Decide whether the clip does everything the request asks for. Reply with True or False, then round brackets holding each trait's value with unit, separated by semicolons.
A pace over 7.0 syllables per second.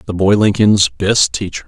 False (4.6 syllables/s)